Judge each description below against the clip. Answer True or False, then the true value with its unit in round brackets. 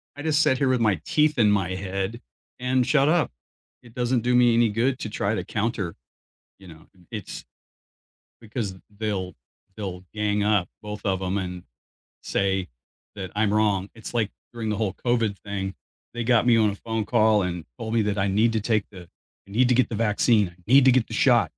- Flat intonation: False (3.3 semitones)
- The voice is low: True (110 Hz)